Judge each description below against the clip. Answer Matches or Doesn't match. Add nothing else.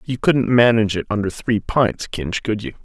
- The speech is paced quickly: Matches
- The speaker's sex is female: Doesn't match